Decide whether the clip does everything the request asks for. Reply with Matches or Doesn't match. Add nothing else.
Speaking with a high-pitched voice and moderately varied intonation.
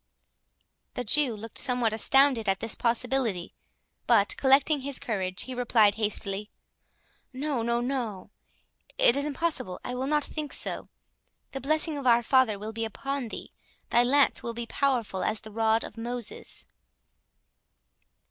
Matches